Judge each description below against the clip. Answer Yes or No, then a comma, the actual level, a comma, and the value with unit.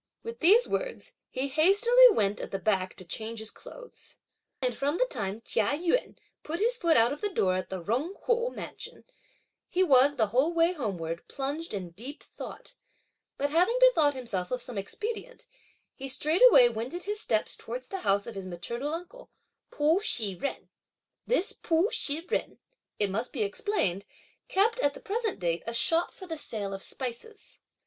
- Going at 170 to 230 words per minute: Yes, average, 180 wpm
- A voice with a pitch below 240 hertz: No, very high, 280 Hz